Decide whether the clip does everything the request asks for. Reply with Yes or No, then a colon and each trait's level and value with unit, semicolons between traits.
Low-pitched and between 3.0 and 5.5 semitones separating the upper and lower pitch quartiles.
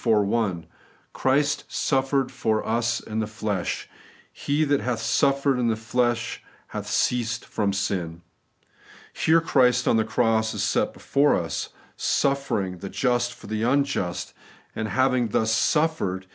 Yes: low, 120 Hz; average, 3.7 semitones